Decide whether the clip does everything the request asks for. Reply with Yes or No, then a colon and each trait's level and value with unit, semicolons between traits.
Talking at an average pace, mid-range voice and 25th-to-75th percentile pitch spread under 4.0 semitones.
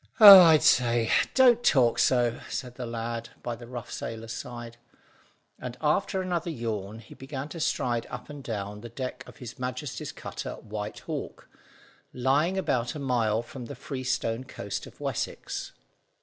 No: average, 160 wpm; low, 125 Hz; average, 3.5 semitones